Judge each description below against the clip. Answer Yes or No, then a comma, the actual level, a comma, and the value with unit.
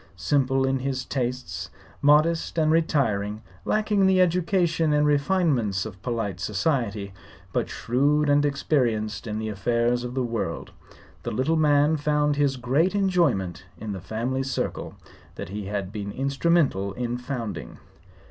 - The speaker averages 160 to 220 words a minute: No, average, 140 wpm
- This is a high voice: No, low, 130 Hz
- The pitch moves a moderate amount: No, wide, 5.7 semitones